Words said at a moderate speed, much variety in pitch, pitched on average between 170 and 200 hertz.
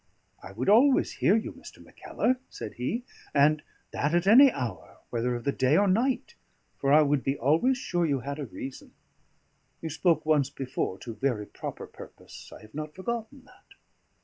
No: average, 180 wpm; wide, 7.5 semitones; medium, 150 Hz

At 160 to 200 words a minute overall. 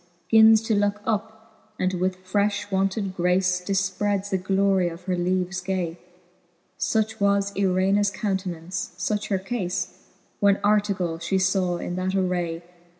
No: average, 140 wpm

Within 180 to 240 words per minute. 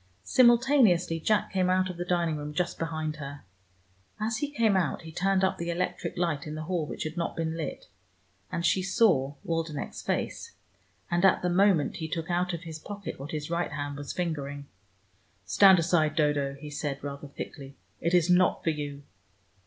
Yes: average, 190 wpm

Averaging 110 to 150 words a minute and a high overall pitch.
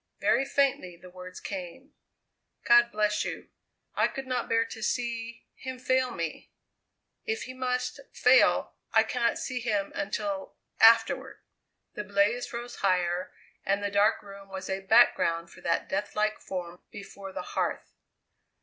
Yes: average, 145 wpm; high, 210 Hz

